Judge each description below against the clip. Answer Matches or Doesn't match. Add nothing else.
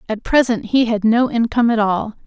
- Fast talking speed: Matches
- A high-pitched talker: Matches